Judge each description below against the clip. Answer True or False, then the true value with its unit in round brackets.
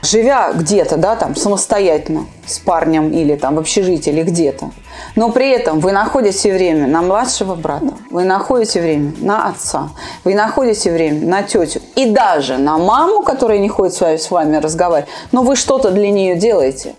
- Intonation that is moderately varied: False (5.8 semitones)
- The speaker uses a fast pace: True (175 wpm)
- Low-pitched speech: False (190 Hz)